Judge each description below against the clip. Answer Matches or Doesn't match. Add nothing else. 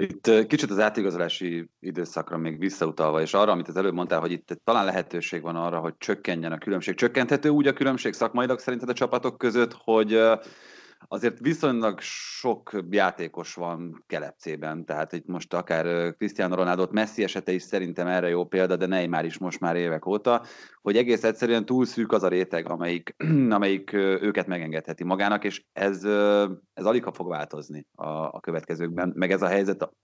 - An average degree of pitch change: Matches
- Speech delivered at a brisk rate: Matches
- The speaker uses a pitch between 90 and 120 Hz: Matches